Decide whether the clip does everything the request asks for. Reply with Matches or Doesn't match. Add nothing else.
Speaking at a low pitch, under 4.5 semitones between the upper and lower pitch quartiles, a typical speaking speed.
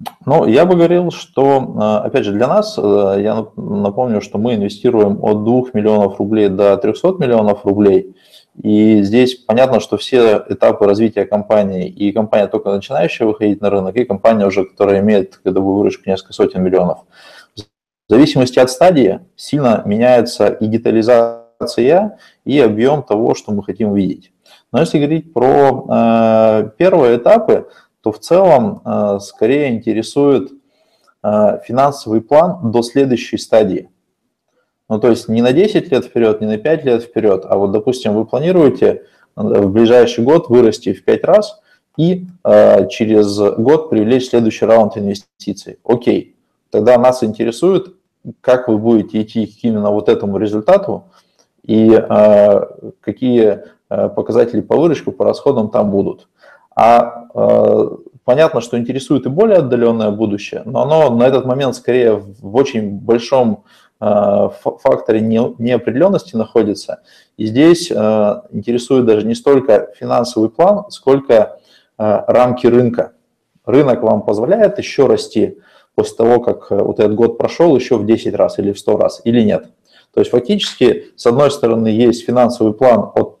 Matches